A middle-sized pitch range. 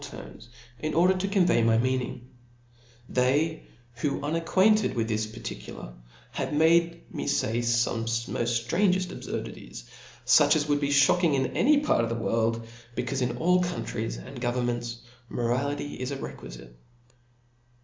No: wide, 6.0 semitones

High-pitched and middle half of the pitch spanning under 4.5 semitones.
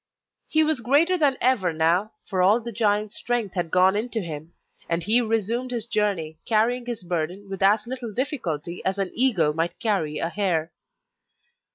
No: high, 205 Hz; wide, 5.6 semitones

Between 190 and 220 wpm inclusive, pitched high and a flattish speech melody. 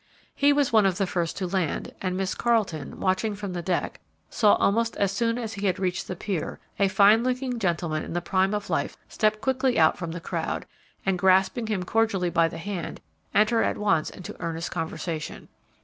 No: average, 200 wpm; high, 195 Hz; average, 3.9 semitones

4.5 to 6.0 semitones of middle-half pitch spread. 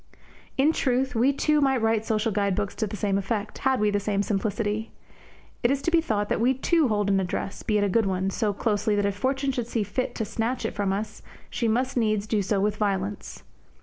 No: average, 3.4 semitones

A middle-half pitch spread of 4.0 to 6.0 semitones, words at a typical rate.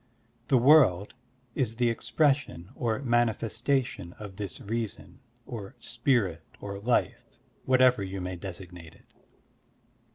No: average, 4.5 semitones; slow, 110 wpm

